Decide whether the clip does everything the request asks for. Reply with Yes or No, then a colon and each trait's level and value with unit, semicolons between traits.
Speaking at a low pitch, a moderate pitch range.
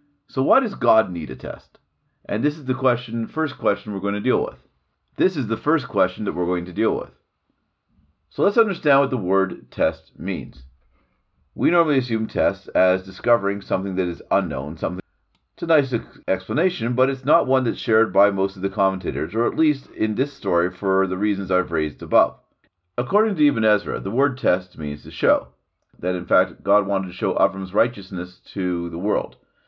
No: low, 100 Hz; wide, 5.8 semitones